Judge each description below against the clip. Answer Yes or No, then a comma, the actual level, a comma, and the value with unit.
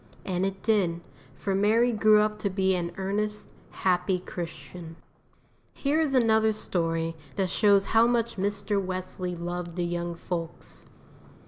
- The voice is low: No, high, 190 Hz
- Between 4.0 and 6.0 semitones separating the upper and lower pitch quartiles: No, average, 3.3 semitones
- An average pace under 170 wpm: Yes, average, 140 wpm